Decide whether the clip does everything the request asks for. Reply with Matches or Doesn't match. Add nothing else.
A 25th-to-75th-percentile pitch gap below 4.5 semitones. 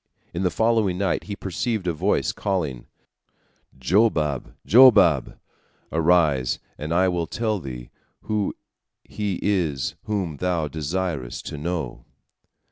Doesn't match